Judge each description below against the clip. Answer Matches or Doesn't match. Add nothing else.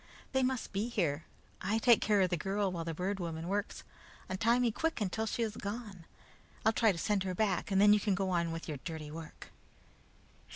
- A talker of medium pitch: Doesn't match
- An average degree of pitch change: Matches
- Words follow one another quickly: Matches